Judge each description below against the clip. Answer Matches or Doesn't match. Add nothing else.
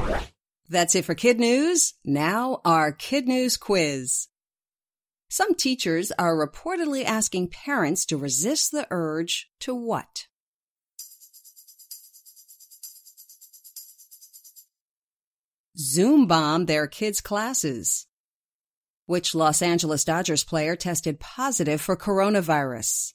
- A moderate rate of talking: Doesn't match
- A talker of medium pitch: Matches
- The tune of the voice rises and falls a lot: Matches